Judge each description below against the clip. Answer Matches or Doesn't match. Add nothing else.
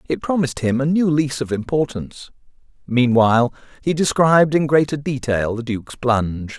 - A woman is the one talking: Doesn't match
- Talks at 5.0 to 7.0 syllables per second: Matches